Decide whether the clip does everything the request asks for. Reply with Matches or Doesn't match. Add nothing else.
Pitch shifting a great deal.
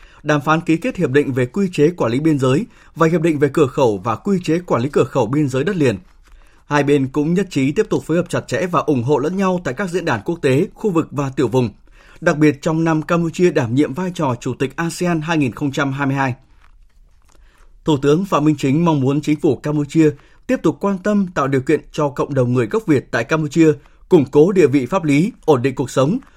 Doesn't match